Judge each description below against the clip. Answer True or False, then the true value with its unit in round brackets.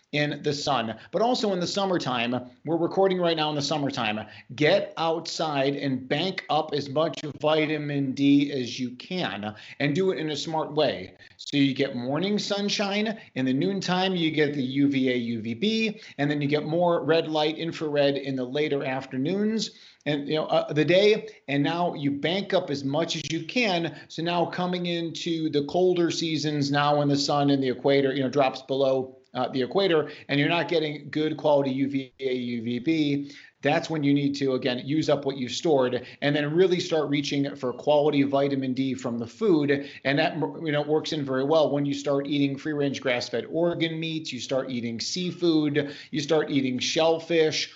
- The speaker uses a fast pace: False (190 wpm)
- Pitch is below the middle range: False (150 Hz)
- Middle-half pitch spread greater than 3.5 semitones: False (3.1 semitones)